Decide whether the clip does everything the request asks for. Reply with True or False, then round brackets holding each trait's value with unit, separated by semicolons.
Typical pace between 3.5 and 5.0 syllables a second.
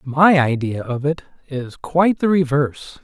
True (4.6 syllables/s)